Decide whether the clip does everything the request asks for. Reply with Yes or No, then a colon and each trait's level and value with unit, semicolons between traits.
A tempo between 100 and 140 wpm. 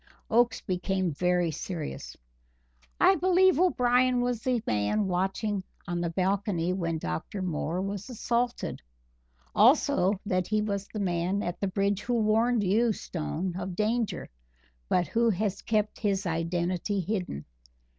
Yes: slow, 135 wpm